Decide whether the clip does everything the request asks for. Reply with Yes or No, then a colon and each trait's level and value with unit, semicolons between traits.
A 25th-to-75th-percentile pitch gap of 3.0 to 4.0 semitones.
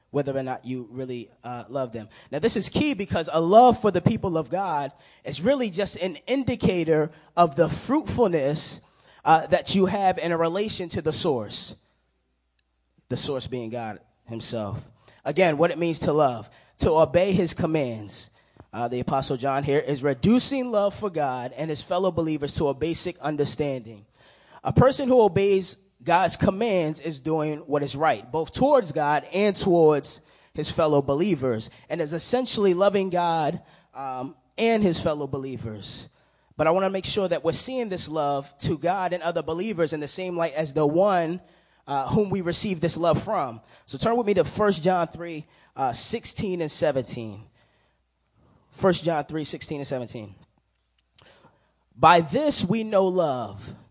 No: wide, 5.6 semitones